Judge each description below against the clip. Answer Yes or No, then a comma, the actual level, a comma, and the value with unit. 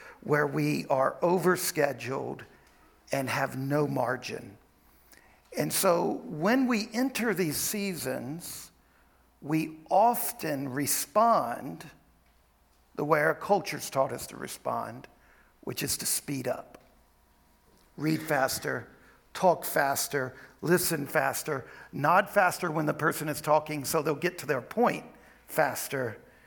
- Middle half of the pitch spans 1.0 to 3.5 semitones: No, average, 4.3 semitones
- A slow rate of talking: Yes, slow, 115 wpm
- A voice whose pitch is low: No, medium, 150 Hz